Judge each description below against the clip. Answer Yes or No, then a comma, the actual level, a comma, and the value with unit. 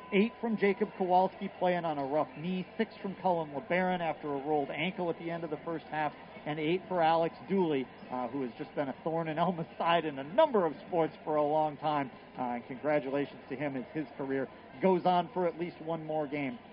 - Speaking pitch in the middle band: Yes, medium, 165 Hz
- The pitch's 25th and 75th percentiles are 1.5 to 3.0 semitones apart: No, average, 3.5 semitones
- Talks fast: Yes, fast, 230 wpm